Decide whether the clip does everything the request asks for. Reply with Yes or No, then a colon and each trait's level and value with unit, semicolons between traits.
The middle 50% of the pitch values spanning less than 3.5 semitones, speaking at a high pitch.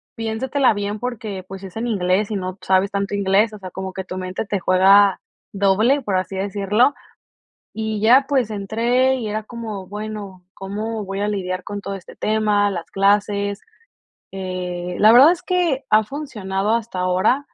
Yes: narrow, 2.6 semitones; high, 205 Hz